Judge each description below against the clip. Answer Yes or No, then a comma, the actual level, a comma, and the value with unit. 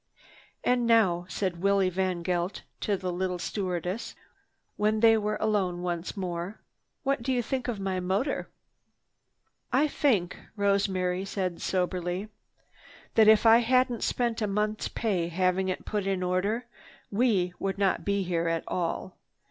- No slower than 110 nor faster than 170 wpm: Yes, average, 145 wpm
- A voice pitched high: Yes, high, 195 Hz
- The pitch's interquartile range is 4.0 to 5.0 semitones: No, average, 3.2 semitones